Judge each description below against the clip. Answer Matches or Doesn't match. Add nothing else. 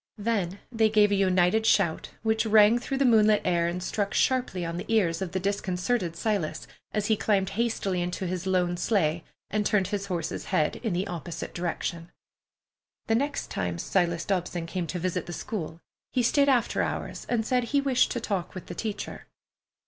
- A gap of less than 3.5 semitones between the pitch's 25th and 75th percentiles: Doesn't match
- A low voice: Doesn't match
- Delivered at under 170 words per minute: Doesn't match